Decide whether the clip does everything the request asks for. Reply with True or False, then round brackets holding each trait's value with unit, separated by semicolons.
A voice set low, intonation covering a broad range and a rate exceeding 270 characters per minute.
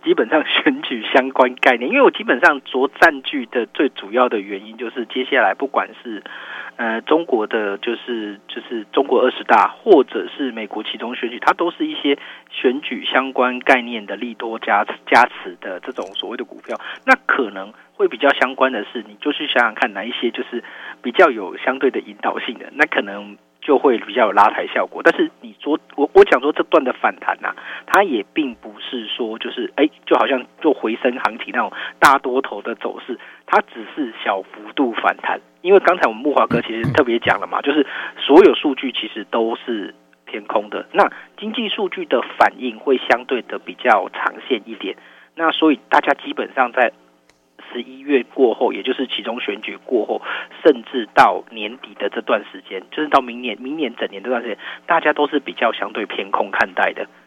True (130 Hz; 5.7 semitones; 290 characters per minute)